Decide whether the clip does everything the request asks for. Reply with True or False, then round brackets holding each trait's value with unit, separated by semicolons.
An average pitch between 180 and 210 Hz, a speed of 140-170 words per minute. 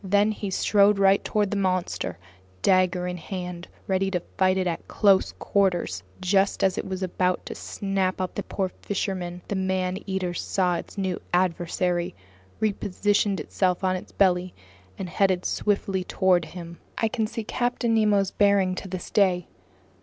True (190 Hz; 160 wpm)